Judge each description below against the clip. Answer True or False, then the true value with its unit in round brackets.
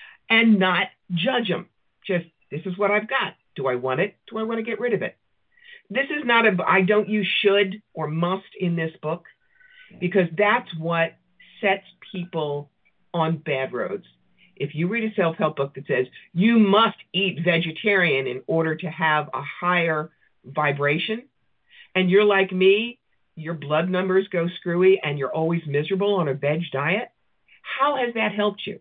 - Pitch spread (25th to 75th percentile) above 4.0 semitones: True (4.7 semitones)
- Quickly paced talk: False (175 wpm)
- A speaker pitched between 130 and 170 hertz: False (185 Hz)